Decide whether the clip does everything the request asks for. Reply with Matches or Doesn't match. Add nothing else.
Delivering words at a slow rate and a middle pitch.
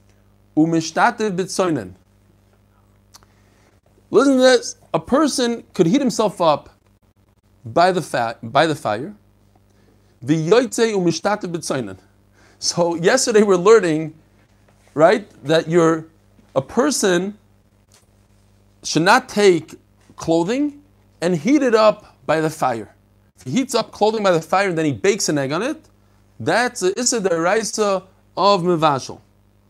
Matches